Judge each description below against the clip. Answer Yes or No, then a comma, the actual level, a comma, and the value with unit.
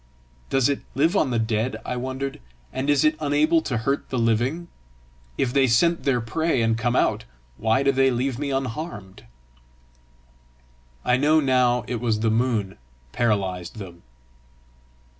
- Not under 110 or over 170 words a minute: Yes, average, 160 wpm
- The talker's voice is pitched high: No, low, 125 Hz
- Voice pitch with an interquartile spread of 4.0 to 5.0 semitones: No, average, 3.4 semitones